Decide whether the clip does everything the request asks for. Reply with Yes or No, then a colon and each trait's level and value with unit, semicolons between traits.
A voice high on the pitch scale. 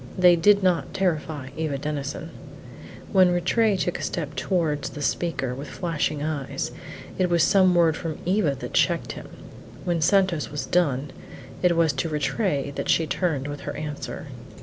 No: medium, 165 Hz